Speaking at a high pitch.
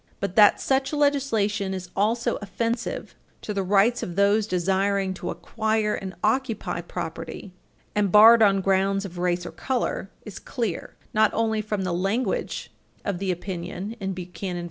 Yes: high, 200 Hz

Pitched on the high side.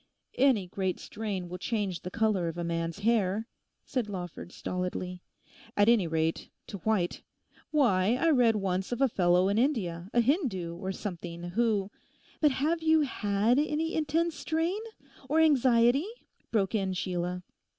Yes: high, 205 Hz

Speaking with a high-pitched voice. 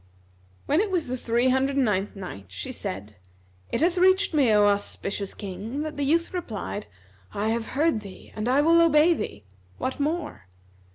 Yes: very high, 260 Hz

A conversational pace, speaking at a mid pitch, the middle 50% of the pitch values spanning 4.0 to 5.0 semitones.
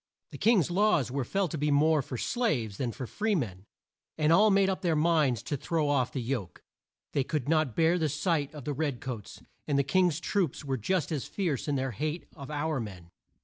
No: fast, 220 wpm; medium, 150 Hz; average, 4.3 semitones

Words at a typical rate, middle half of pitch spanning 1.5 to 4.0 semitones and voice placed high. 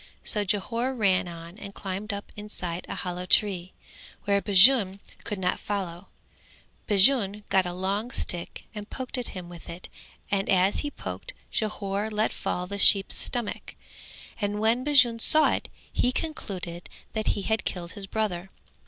Yes: average, 160 wpm; average, 3.0 semitones; high, 200 Hz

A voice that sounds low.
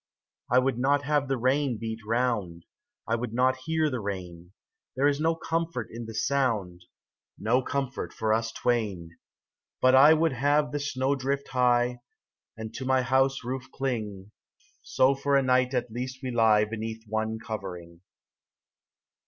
Yes: low, 125 Hz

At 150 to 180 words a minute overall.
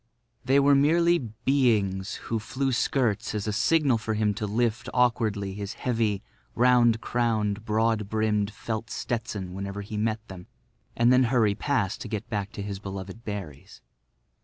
Yes: average, 160 wpm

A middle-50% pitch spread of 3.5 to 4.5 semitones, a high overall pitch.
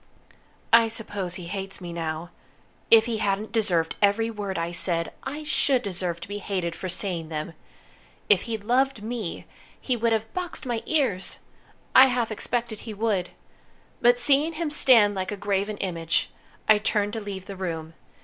Yes: average, 4.1 semitones; high, 205 Hz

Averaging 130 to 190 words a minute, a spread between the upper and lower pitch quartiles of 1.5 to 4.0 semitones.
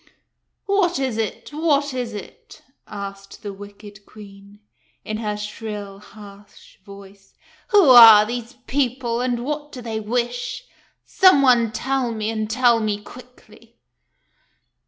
Yes: average, 140 wpm; average, 3.3 semitones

